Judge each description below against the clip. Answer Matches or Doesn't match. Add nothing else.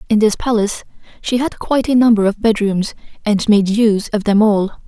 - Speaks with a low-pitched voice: Doesn't match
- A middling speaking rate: Matches